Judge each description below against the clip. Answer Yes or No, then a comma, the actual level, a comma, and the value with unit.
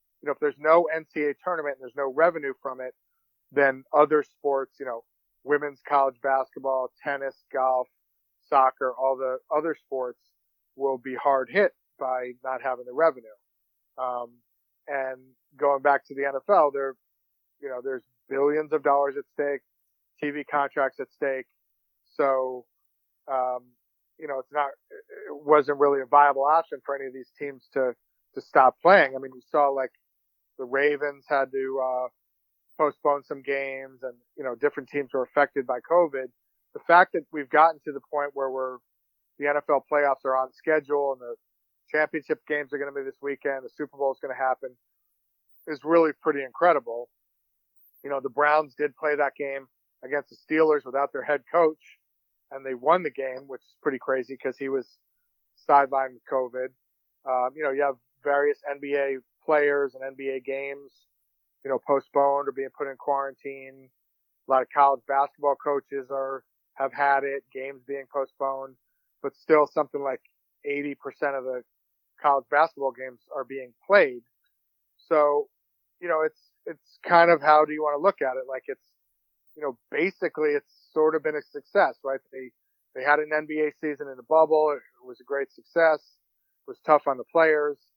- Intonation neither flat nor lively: No, narrow, 2.1 semitones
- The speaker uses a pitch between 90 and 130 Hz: No, medium, 140 Hz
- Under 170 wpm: No, average, 175 wpm